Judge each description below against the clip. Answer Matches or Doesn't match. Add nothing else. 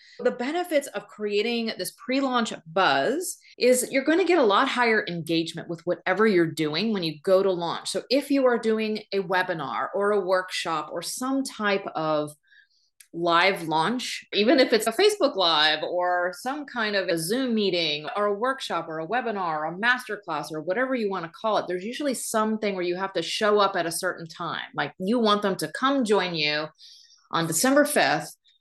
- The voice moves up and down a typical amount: Doesn't match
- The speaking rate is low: Doesn't match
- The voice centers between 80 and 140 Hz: Doesn't match